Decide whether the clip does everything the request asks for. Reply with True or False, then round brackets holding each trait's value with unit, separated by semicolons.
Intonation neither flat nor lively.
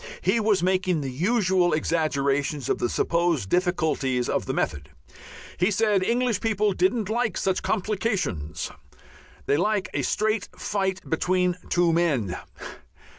True (5.0 semitones)